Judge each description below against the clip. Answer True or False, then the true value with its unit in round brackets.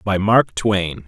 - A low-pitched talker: True (100 Hz)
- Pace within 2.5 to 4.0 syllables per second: True (3.1 syllables/s)